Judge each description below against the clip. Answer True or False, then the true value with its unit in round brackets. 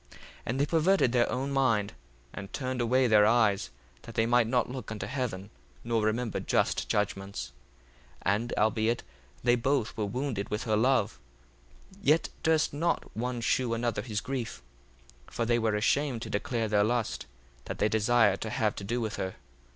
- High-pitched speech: False (115 Hz)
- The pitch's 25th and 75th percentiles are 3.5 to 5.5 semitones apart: False (3.0 semitones)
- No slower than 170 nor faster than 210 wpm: True (180 wpm)